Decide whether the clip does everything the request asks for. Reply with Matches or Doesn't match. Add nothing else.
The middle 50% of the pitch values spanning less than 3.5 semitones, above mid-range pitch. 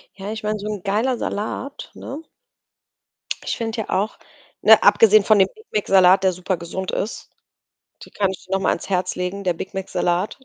Matches